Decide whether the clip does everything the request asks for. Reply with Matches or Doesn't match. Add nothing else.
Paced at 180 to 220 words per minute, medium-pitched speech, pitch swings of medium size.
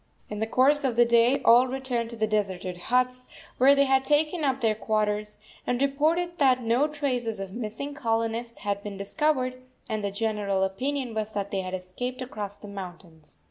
Doesn't match